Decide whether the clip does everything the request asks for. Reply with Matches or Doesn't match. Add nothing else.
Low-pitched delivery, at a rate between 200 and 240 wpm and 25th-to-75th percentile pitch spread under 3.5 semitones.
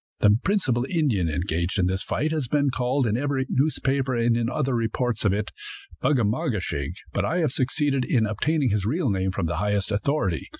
Doesn't match